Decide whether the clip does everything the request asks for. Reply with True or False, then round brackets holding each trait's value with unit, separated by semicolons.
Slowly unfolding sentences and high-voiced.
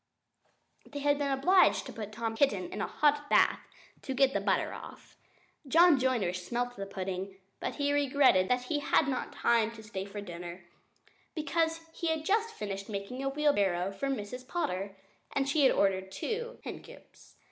False (180 wpm; 250 Hz)